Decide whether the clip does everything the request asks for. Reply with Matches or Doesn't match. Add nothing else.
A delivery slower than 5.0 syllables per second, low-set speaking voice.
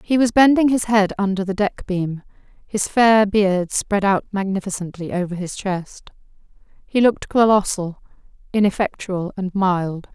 Doesn't match